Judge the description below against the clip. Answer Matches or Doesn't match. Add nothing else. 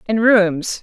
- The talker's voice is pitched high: Matches